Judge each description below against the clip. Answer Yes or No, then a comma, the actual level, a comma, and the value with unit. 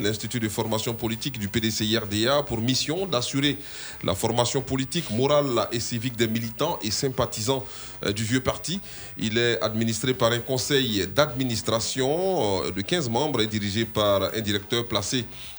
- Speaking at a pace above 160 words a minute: No, slow, 145 wpm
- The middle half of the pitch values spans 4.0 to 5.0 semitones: No, average, 3.2 semitones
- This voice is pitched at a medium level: No, low, 120 Hz